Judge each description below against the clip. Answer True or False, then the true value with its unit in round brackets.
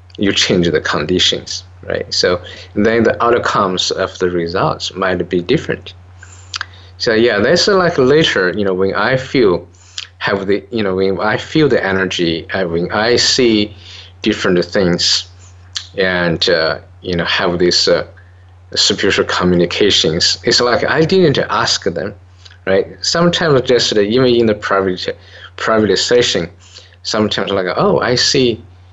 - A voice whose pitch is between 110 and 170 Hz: False (95 Hz)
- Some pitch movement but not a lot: False (2.3 semitones)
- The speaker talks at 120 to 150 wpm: True (145 wpm)